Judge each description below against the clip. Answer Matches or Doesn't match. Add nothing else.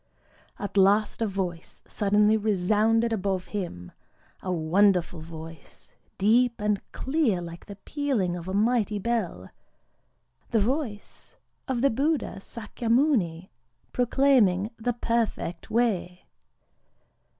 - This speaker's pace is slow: Matches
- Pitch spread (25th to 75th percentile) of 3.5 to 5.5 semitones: Matches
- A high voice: Matches